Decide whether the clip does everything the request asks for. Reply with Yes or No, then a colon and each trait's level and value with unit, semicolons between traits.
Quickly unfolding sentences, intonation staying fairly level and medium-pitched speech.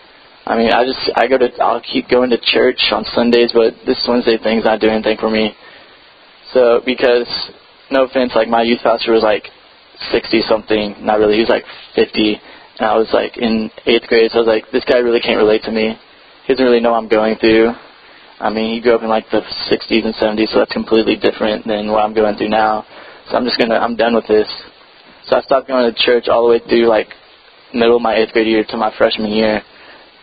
No: fast, 235 wpm; narrow, 1.4 semitones; low, 115 Hz